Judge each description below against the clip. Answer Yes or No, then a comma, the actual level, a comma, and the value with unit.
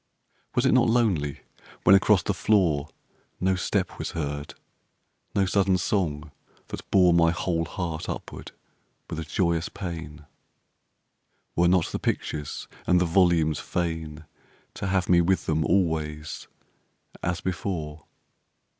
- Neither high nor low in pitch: No, very low, 85 Hz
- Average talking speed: No, slow, 130 wpm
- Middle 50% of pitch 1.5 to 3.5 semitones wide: Yes, average, 3.2 semitones